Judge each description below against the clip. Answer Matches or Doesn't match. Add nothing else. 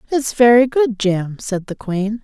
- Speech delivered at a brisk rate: Doesn't match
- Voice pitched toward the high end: Matches